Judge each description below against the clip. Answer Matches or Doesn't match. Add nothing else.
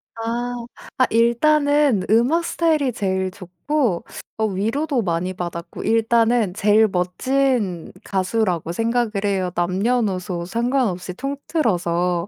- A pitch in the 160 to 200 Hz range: Doesn't match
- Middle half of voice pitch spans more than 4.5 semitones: Matches